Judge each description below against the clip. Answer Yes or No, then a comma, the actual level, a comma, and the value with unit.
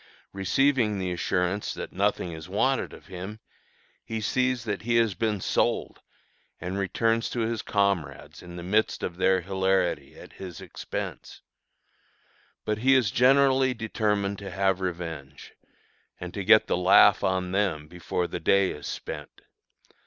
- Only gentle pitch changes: No, average, 3.7 semitones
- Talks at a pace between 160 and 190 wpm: No, average, 150 wpm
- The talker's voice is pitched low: Yes, low, 100 Hz